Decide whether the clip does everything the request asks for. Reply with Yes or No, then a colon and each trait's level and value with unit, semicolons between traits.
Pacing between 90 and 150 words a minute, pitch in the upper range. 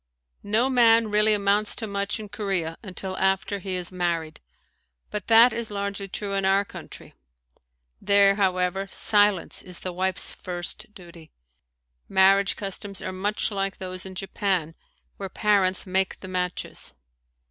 Yes: average, 145 wpm; high, 195 Hz